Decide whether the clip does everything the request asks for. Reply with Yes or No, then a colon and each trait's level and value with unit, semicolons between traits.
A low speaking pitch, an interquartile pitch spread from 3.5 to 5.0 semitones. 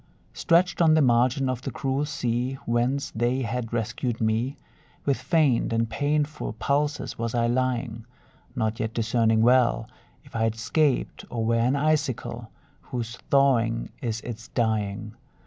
No: low, 120 Hz; average, 3.1 semitones